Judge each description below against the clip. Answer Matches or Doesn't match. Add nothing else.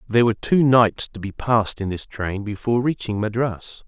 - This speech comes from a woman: Doesn't match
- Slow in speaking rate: Doesn't match